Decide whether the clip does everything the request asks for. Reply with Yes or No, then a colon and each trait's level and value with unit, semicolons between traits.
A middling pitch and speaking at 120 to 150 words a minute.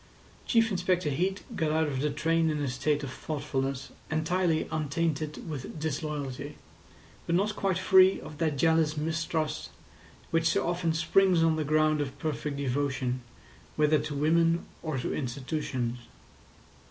Yes: medium, 155 Hz; average, 145 wpm